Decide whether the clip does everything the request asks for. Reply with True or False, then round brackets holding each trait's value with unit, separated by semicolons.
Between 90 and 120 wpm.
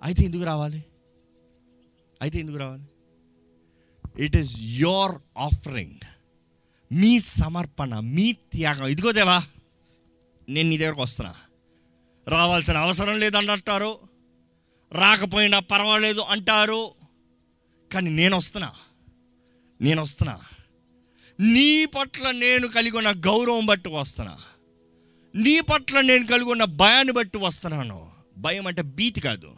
True (100 wpm)